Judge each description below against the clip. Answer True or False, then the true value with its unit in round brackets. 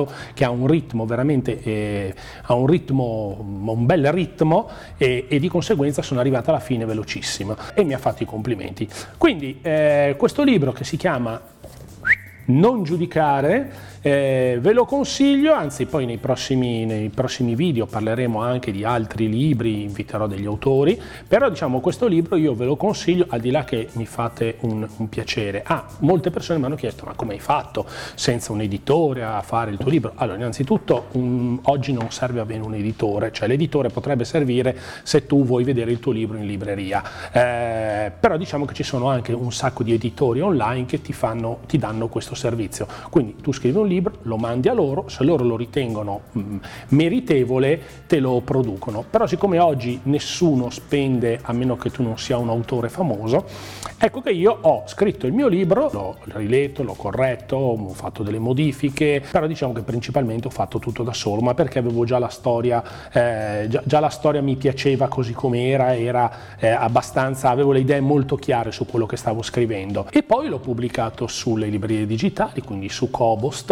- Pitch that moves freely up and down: False (4.1 semitones)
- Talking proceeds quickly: True (185 wpm)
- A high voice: False (125 Hz)